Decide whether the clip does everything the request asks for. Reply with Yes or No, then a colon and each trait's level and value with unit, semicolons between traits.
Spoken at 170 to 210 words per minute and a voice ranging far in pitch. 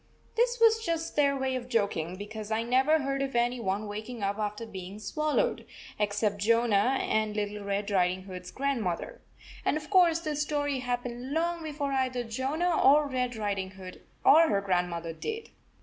Yes: average, 175 wpm; wide, 6.3 semitones